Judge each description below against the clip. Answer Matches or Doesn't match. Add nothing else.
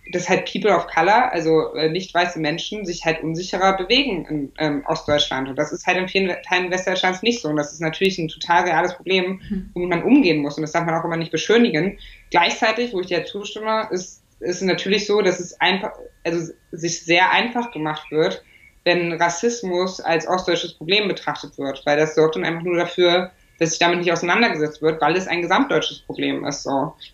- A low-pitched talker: Doesn't match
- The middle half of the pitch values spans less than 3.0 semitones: Matches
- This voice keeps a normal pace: Doesn't match